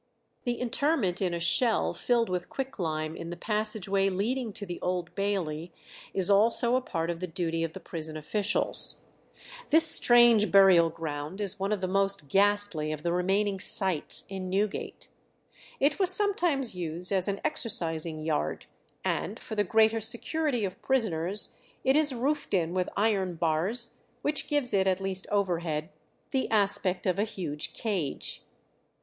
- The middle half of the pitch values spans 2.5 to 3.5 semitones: No, average, 4.6 semitones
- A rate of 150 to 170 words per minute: Yes, average, 160 wpm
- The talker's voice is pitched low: No, high, 195 Hz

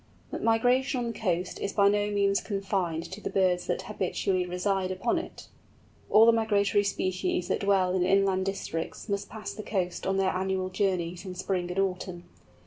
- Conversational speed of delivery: Yes, average, 185 wpm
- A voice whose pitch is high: Yes, high, 195 Hz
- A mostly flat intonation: Yes, narrow, 1.9 semitones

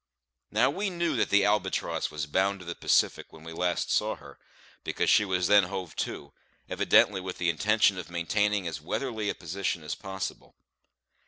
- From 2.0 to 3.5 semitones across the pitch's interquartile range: Yes, average, 3.2 semitones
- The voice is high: No, very low, 95 Hz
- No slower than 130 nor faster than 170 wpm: No, average, 180 wpm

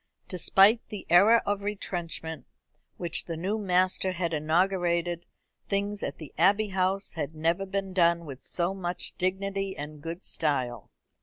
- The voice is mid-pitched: Yes, medium, 180 Hz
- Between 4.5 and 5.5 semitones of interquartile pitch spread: No, average, 3.0 semitones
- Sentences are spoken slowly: No, average, 145 wpm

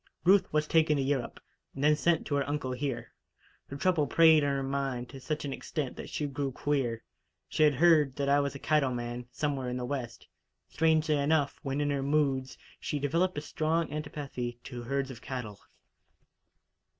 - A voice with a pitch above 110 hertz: Yes, medium, 140 Hz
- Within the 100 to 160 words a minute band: No, average, 190 wpm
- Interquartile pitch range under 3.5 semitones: Yes, narrow, 2.5 semitones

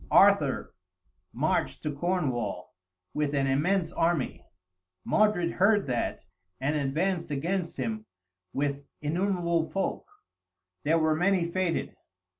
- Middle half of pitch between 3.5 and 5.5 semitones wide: Yes, average, 4.6 semitones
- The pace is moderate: No, slow, 105 wpm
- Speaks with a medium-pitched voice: Yes, medium, 165 Hz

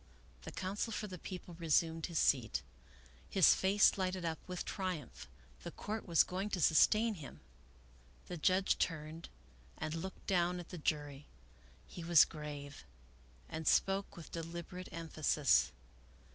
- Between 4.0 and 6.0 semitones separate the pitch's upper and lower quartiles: No, average, 3.2 semitones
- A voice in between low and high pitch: Yes, medium, 170 Hz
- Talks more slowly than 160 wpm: Yes, average, 140 wpm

